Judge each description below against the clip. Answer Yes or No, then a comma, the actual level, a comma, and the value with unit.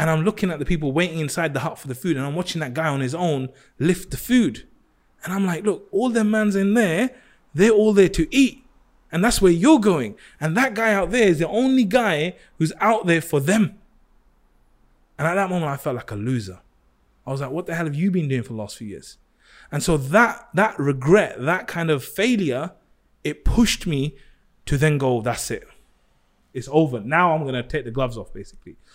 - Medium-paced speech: No, fast, 225 wpm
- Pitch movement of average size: No, wide, 6.7 semitones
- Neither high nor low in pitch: Yes, medium, 165 Hz